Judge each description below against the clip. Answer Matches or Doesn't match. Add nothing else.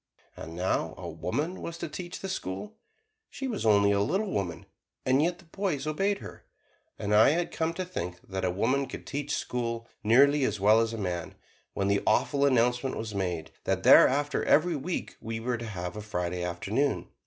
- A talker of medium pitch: Doesn't match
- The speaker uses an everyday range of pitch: Doesn't match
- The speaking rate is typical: Matches